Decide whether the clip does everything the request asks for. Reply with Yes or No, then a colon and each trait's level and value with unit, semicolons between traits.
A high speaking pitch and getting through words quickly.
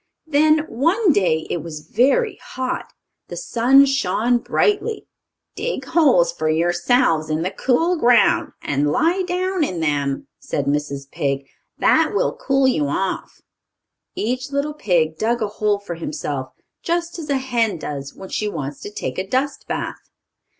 No: high, 225 Hz; average, 155 wpm